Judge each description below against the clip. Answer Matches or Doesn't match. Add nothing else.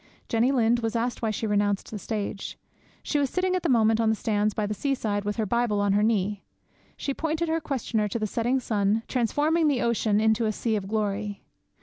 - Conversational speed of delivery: Doesn't match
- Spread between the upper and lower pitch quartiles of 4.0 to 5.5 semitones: Doesn't match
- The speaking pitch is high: Matches